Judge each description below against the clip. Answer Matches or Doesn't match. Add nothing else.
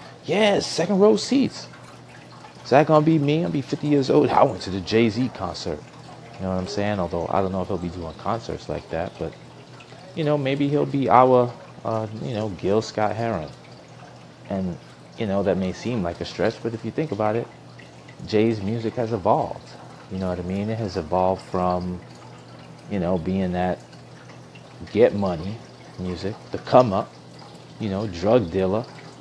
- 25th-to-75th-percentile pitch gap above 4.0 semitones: Matches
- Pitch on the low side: Matches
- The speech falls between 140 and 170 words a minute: Doesn't match